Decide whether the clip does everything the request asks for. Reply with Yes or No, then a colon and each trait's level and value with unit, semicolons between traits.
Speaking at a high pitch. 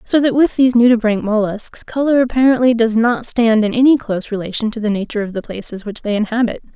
Yes: high, 230 Hz